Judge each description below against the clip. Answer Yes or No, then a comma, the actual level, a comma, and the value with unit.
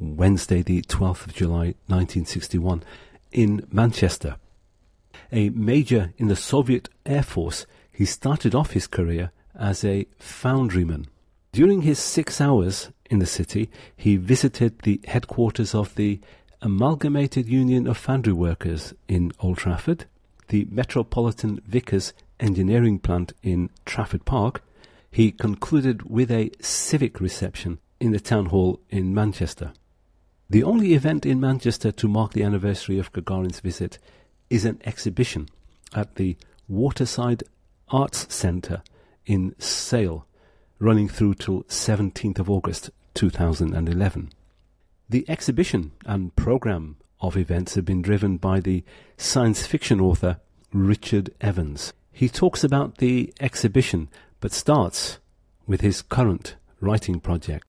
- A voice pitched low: Yes, low, 100 Hz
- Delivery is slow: Yes, slow, 125 wpm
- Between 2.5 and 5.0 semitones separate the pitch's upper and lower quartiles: Yes, average, 4.7 semitones